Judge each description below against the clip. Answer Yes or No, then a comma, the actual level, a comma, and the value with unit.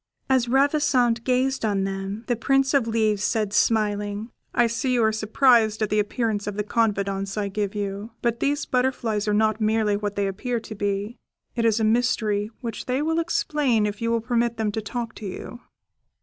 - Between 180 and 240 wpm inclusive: Yes, average, 195 wpm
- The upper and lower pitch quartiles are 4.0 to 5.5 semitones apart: No, average, 2.7 semitones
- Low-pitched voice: No, high, 220 Hz